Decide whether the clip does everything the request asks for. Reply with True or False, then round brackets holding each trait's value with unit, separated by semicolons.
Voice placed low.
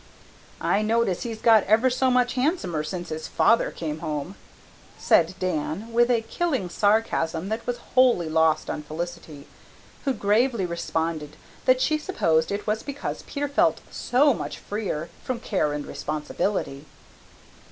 False (200 Hz)